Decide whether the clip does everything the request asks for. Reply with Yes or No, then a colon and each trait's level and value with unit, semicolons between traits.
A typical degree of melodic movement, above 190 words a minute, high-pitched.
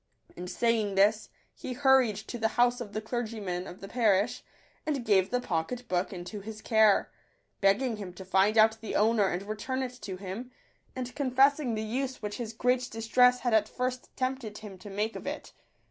Yes: average, 3.7 semitones; average, 200 wpm; high, 220 Hz